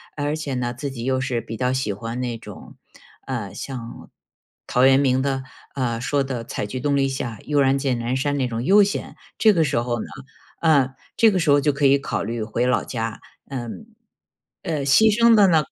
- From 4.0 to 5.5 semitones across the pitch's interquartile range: No, average, 3.1 semitones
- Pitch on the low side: Yes, low, 130 Hz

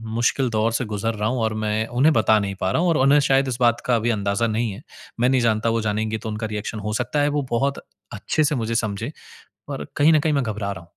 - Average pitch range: Yes, average, 3.5 semitones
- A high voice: No, low, 115 Hz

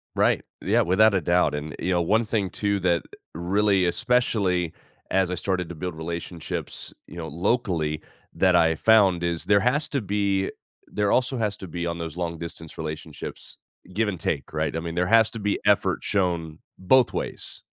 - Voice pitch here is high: No, very low, 90 Hz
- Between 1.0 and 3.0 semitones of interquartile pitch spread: No, average, 3.5 semitones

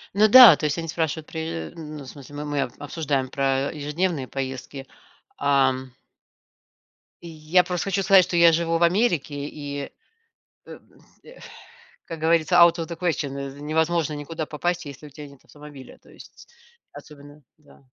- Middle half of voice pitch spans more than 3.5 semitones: No, average, 2.9 semitones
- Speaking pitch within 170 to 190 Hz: No, medium, 155 Hz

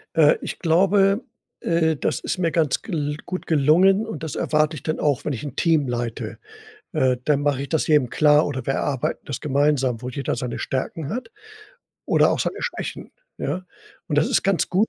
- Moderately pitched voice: Yes, medium, 150 Hz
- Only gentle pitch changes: No, average, 3.7 semitones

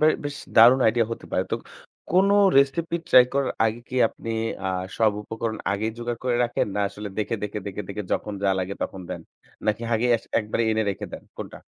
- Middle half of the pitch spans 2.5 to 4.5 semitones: Yes, average, 2.8 semitones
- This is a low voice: Yes, low, 115 Hz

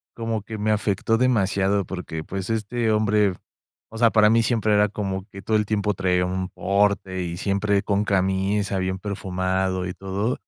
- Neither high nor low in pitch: No, low, 100 Hz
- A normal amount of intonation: No, narrow, 2.1 semitones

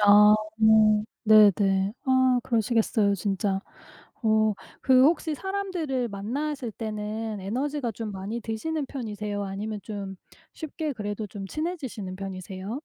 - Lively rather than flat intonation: No, average, 4.3 semitones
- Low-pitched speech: No, high, 220 Hz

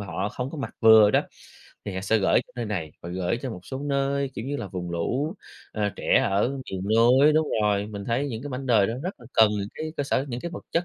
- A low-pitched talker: Yes, low, 115 Hz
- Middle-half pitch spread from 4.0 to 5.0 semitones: No, wide, 5.4 semitones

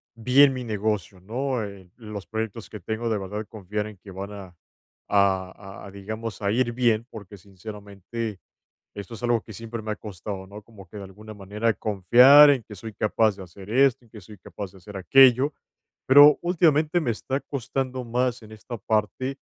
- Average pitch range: Yes, average, 3.3 semitones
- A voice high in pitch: No, low, 110 Hz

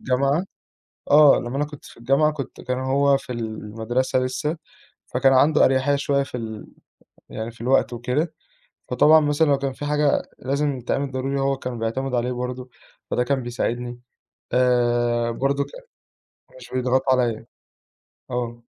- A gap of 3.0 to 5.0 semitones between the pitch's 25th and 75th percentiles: No, narrow, 2.5 semitones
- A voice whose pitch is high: No, low, 130 Hz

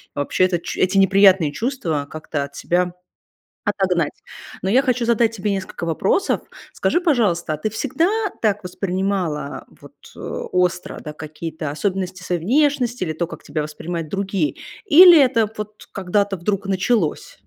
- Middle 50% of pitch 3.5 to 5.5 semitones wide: Yes, average, 4.4 semitones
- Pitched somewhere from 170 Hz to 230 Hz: Yes, high, 190 Hz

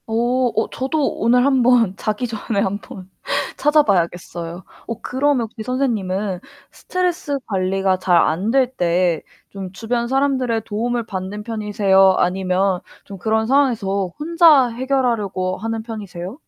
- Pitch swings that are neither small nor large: Yes, average, 4.8 semitones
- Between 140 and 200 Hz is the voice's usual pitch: No, high, 220 Hz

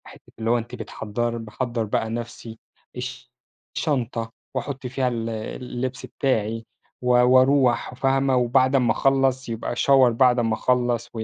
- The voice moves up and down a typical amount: No, narrow, 2.1 semitones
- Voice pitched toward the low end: Yes, low, 125 Hz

